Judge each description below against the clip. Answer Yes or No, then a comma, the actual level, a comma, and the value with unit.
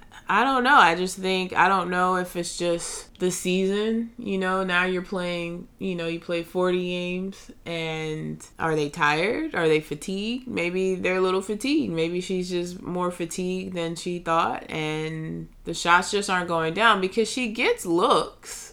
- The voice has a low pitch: No, medium, 180 Hz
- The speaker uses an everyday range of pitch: No, narrow, 2.2 semitones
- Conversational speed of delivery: Yes, average, 180 wpm